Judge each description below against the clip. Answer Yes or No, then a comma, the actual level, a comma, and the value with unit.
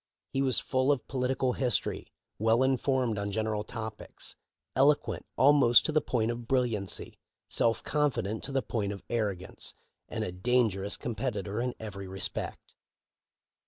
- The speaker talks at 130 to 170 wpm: Yes, average, 140 wpm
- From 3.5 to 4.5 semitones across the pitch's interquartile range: Yes, average, 3.9 semitones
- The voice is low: Yes, low, 120 Hz